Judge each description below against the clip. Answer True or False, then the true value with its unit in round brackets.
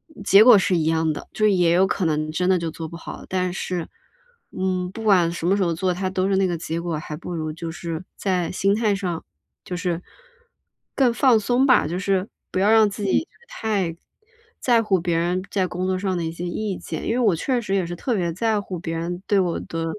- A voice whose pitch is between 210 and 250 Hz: False (185 Hz)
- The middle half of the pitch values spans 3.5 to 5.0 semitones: False (2.9 semitones)